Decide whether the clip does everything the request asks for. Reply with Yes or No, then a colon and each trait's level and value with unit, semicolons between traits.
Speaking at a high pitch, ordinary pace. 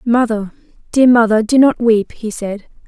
Yes: high, 230 Hz; average, 165 wpm